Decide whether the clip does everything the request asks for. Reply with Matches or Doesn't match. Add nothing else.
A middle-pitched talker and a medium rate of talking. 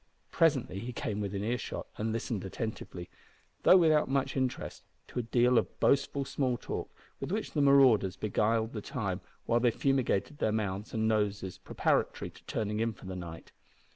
Doesn't match